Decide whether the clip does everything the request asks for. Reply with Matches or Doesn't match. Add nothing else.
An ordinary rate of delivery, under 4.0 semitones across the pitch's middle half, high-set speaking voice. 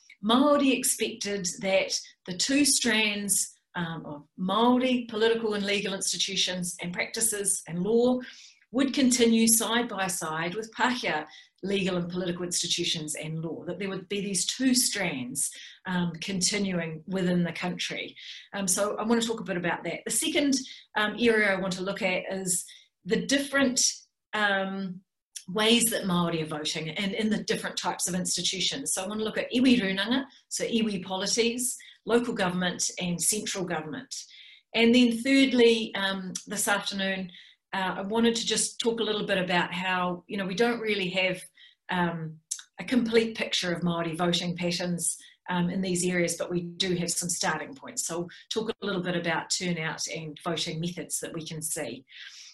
Doesn't match